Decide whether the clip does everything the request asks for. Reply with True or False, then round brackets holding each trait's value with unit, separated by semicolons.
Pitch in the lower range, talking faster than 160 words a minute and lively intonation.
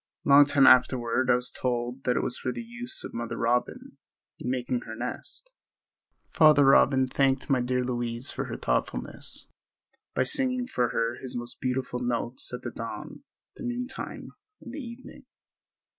False (130 Hz; 175 wpm; 3.0 semitones)